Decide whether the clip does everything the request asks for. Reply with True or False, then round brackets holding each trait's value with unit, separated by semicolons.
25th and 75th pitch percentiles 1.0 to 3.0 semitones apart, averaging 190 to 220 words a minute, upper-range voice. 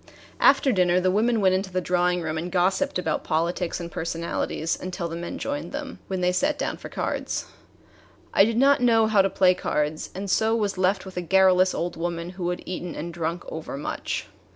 False (2.6 semitones; 205 wpm; 180 Hz)